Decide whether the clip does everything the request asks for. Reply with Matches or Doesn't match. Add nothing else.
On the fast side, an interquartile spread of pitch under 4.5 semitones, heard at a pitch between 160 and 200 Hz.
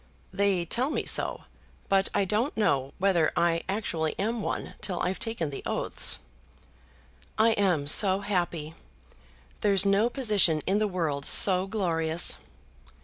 Doesn't match